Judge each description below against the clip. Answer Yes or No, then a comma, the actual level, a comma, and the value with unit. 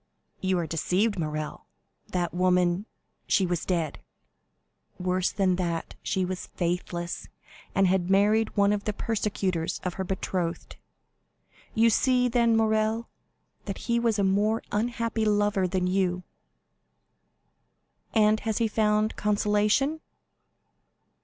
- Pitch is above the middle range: Yes, high, 200 Hz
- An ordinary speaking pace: No, slow, 120 wpm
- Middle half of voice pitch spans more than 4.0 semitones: No, average, 3.2 semitones